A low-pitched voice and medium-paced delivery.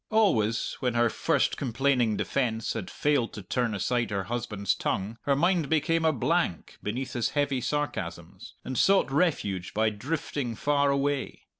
Yes: low, 125 Hz; average, 155 wpm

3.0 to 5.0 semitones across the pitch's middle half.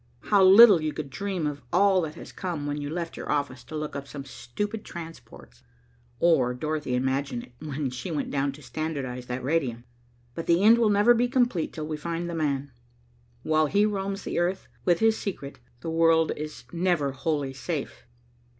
Yes: average, 4.6 semitones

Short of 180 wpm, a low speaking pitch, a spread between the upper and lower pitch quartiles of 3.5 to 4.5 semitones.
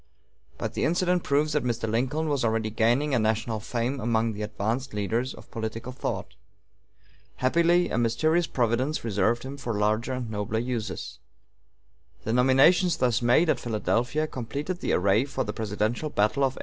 Yes: average, 165 wpm; low, 120 Hz; average, 4.0 semitones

